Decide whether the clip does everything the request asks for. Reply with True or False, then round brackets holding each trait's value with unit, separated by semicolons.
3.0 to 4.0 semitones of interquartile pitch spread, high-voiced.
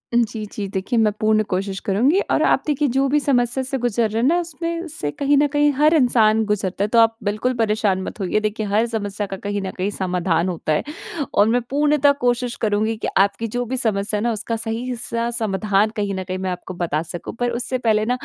True (3.7 semitones; 220 Hz)